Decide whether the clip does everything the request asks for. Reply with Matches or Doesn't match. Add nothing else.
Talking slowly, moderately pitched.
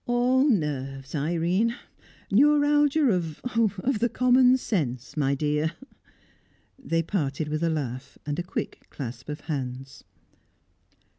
Matches